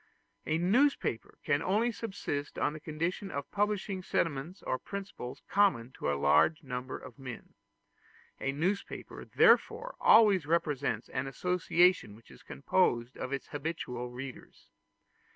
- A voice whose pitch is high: No, medium, 155 Hz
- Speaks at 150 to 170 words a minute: No, slow, 135 wpm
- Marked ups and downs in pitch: Yes, wide, 6.7 semitones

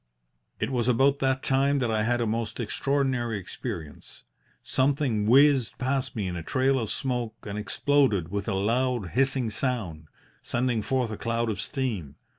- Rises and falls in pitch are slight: No, average, 3.9 semitones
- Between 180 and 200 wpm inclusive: No, average, 165 wpm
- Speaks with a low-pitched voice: Yes, low, 120 Hz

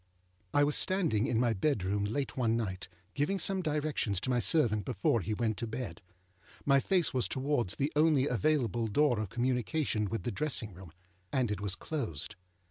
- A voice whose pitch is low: Yes, low, 120 Hz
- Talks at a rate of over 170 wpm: Yes, average, 180 wpm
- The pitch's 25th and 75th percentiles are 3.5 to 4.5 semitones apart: No, wide, 5.5 semitones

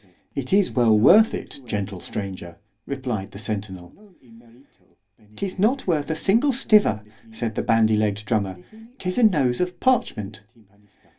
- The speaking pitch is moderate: No, low, 120 Hz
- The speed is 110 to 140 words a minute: Yes, slow, 135 wpm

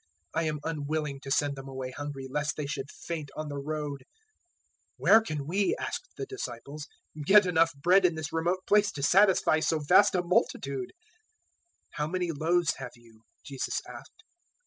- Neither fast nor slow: Yes, average, 175 wpm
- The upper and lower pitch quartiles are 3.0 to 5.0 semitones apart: Yes, average, 3.9 semitones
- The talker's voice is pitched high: No, medium, 150 Hz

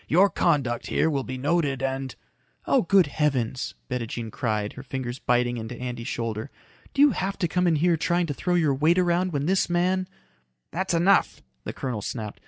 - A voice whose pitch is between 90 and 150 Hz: Yes, medium, 140 Hz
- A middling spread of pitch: No, wide, 6.1 semitones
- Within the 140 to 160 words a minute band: No, average, 195 wpm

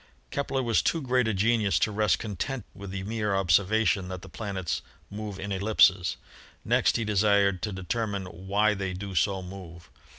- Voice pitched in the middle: No, low, 100 Hz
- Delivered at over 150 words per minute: Yes, average, 170 wpm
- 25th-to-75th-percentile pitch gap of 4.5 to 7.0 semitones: No, narrow, 2.5 semitones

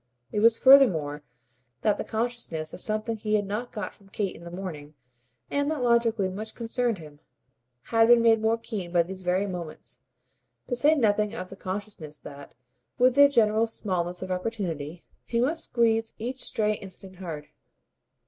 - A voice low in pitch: No, high, 210 Hz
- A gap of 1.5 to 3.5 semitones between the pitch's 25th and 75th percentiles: No, average, 4.4 semitones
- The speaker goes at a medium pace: Yes, average, 170 wpm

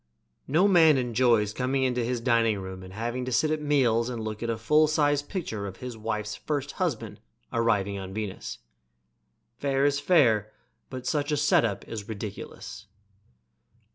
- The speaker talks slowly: No, average, 165 wpm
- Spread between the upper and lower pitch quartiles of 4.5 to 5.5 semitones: Yes, average, 5.0 semitones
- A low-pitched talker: Yes, low, 120 Hz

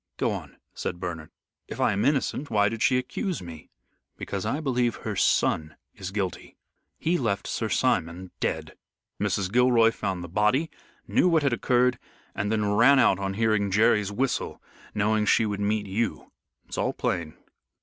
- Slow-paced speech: No, average, 170 wpm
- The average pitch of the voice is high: No, low, 105 Hz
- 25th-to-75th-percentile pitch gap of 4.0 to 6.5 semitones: Yes, average, 4.3 semitones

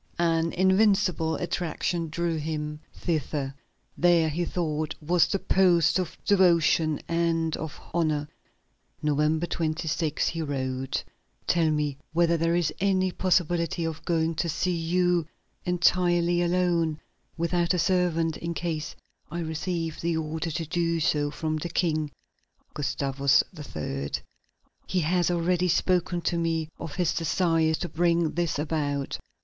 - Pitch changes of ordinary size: No, narrow, 1.9 semitones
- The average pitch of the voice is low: No, medium, 165 Hz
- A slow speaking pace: Yes, slow, 130 wpm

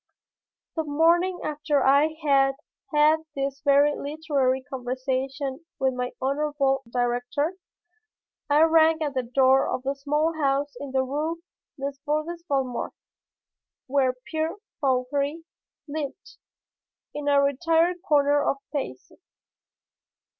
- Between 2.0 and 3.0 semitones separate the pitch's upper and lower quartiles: Yes, narrow, 2.5 semitones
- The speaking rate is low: Yes, slow, 110 wpm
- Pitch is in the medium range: No, very high, 285 Hz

